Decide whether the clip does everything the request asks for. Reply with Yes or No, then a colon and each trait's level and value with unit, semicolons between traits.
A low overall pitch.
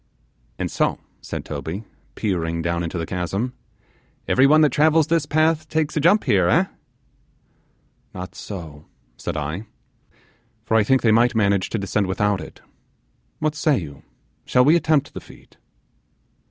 Yes: low, 110 Hz